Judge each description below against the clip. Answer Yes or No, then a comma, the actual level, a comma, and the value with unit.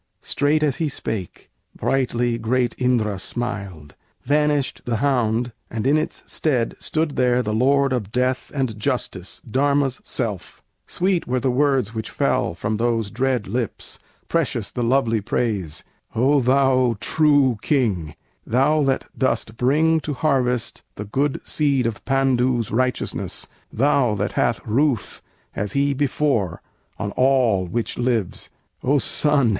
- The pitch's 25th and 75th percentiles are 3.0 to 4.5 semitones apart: Yes, average, 3.8 semitones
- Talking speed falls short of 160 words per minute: Yes, average, 140 wpm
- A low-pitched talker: Yes, low, 125 Hz